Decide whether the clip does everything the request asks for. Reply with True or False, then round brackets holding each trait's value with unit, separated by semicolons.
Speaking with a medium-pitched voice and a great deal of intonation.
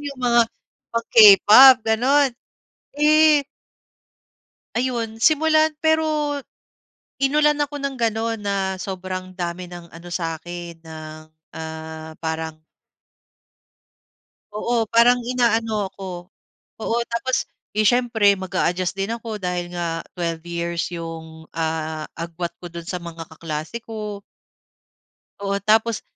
False (200 Hz; 5.8 semitones)